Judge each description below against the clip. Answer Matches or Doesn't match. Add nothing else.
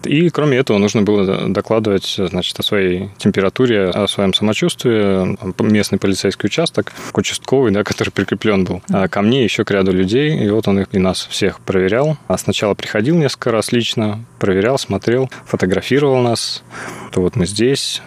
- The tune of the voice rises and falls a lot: Doesn't match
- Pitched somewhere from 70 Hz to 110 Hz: Matches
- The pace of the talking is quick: Matches